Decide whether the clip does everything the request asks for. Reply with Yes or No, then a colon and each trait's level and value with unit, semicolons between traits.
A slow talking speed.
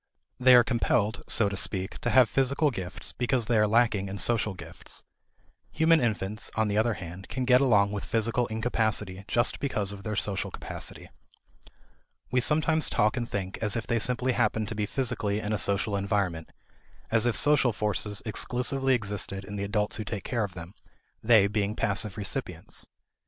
No: average, 180 wpm